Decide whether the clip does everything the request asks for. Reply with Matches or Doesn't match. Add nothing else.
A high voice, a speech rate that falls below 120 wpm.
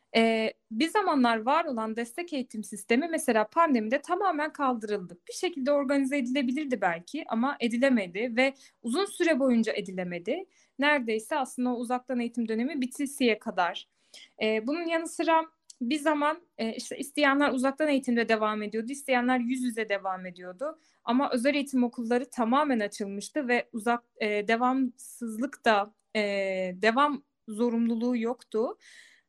Doesn't match